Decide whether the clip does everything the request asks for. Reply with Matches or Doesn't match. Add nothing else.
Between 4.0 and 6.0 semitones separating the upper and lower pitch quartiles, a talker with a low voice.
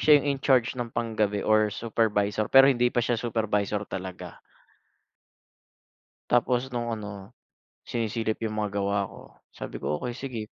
Doesn't match